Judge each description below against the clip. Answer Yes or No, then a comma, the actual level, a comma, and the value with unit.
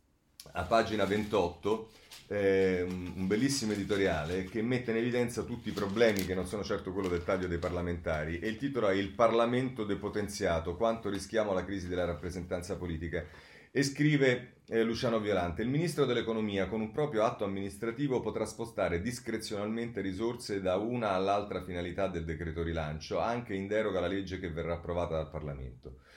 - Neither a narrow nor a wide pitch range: Yes, average, 4.4 semitones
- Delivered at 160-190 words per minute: Yes, average, 165 wpm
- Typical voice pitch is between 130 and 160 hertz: No, low, 100 Hz